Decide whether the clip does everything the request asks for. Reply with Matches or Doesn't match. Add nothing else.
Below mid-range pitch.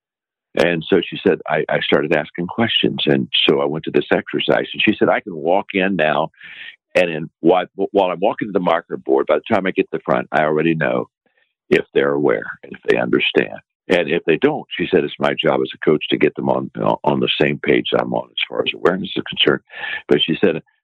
Matches